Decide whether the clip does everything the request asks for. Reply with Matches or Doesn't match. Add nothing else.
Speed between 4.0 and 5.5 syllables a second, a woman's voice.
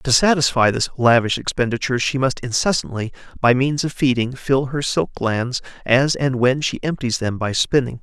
Doesn't match